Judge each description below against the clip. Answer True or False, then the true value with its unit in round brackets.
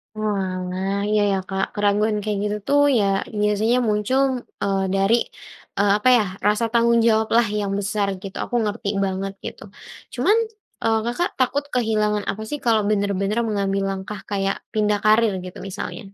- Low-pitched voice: False (210 Hz)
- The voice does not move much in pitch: True (2.1 semitones)